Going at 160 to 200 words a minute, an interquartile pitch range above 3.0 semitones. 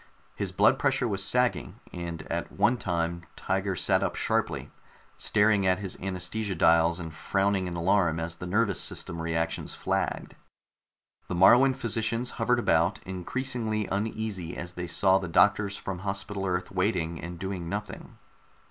No: average, 150 wpm; average, 3.4 semitones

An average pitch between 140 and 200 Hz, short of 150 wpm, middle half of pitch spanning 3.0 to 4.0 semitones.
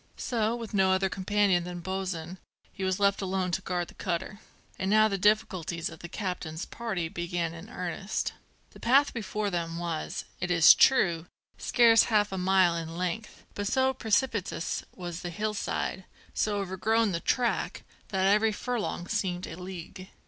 No: high, 190 Hz; average, 165 wpm; average, 3.3 semitones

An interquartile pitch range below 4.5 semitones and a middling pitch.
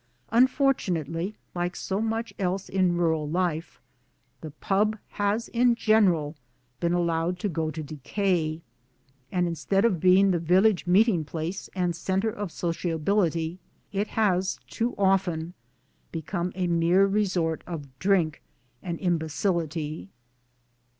Yes: average, 3.3 semitones; medium, 180 Hz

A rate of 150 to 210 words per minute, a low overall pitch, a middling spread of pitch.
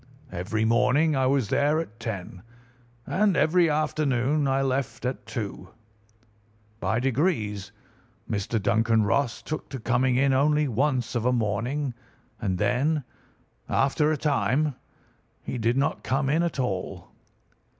No: slow, 135 wpm; low, 130 Hz; average, 4.6 semitones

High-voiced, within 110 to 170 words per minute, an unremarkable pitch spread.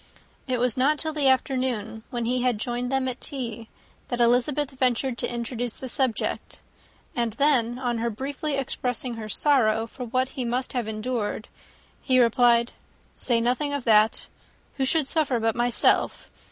No: high, 245 Hz; average, 160 wpm; narrow, 2.1 semitones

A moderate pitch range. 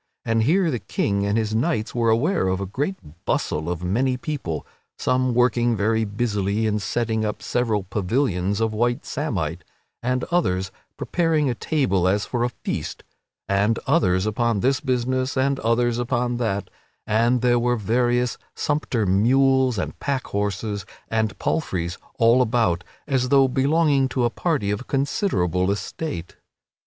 Yes: average, 4.3 semitones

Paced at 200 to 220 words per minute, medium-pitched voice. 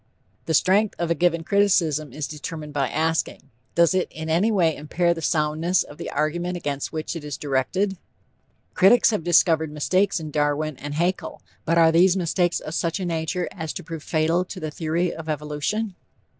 No: average, 185 wpm; medium, 165 Hz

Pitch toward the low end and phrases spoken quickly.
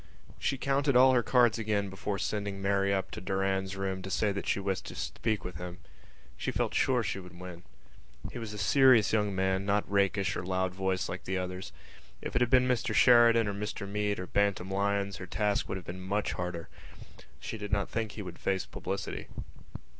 Yes: low, 100 Hz; fast, 210 wpm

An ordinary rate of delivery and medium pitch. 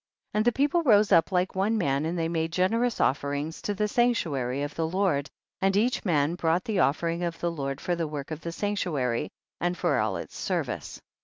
No: fast, 220 wpm; medium, 170 Hz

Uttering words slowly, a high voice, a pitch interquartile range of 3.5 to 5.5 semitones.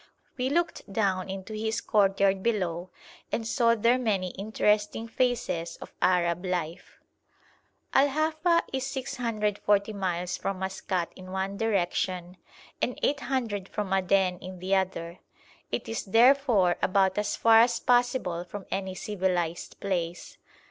Yes: slow, 130 wpm; high, 195 Hz; average, 4.0 semitones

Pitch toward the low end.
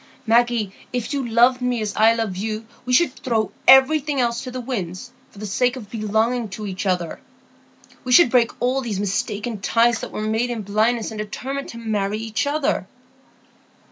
No: high, 230 Hz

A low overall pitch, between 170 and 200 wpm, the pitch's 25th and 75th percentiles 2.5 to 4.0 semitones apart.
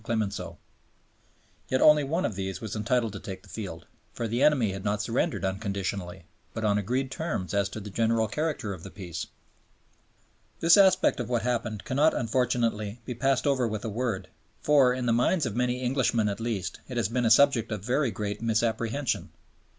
Yes: low, 115 Hz; average, 190 wpm; average, 3.7 semitones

